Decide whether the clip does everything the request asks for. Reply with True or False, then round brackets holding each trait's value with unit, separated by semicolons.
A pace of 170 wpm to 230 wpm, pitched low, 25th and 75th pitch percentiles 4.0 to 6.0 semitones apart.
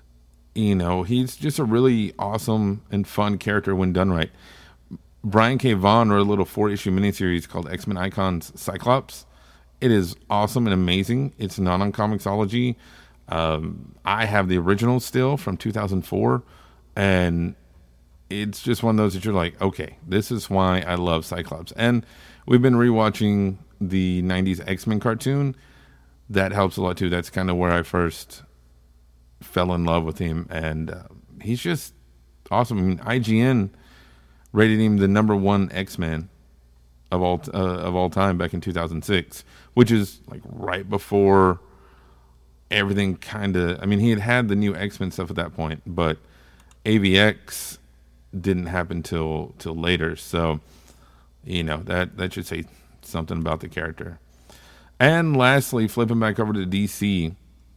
False (160 wpm; 95 Hz; 4.6 semitones)